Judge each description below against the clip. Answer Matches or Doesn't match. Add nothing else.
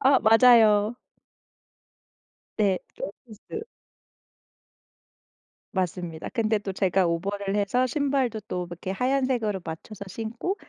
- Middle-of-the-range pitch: Doesn't match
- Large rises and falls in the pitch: Doesn't match